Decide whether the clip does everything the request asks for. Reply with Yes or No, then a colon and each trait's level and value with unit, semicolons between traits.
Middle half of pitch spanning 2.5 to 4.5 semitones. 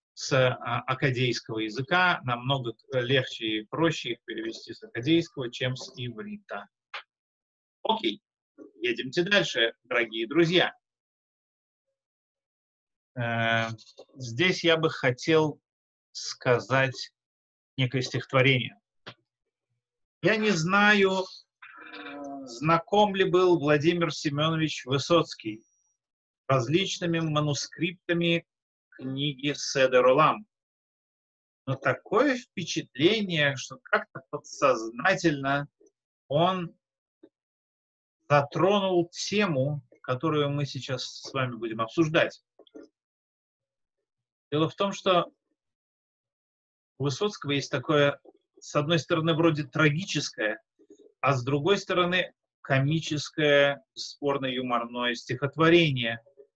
No: average, 5.2 semitones